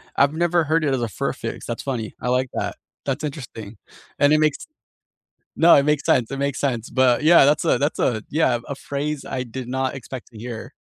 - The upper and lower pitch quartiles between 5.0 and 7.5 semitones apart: No, average, 3.4 semitones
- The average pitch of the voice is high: No, low, 135 Hz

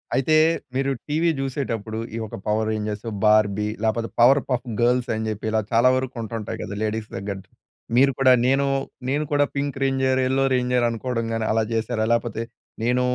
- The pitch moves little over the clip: No, average, 3.3 semitones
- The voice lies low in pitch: Yes, low, 120 Hz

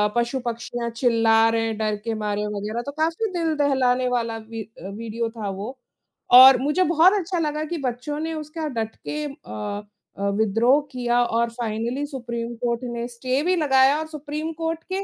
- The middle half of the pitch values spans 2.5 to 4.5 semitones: No, average, 4.9 semitones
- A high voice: Yes, very high, 250 Hz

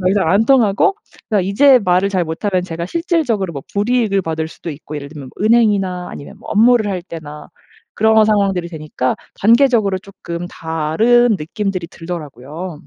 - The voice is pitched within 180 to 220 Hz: Yes, high, 190 Hz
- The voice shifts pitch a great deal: No, average, 5.0 semitones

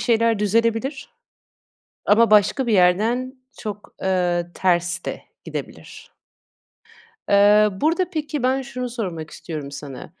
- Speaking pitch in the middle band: No, high, 210 Hz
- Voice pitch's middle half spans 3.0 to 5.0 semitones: No, wide, 5.5 semitones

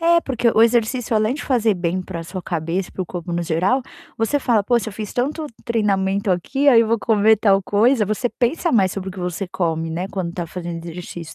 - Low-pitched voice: No, high, 200 Hz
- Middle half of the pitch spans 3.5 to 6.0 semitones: Yes, average, 4.7 semitones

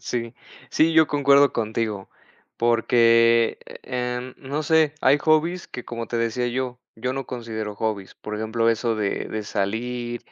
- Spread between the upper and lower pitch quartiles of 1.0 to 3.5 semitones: Yes, average, 2.7 semitones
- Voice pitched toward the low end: Yes, low, 120 Hz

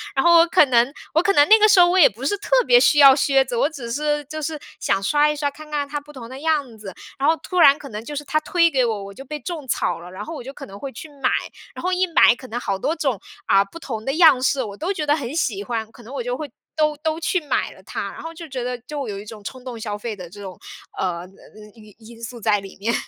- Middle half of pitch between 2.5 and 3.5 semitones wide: No, wide, 5.6 semitones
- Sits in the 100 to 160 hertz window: No, very high, 270 Hz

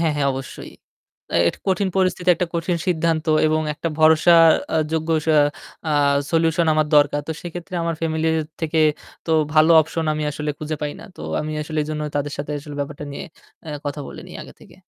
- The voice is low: No, medium, 155 Hz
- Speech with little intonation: Yes, narrow, 1.9 semitones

